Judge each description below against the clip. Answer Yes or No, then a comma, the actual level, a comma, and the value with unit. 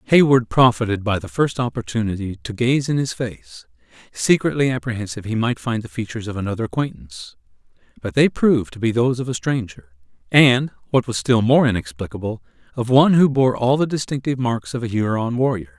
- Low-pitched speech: Yes, low, 120 Hz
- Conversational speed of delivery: Yes, average, 180 wpm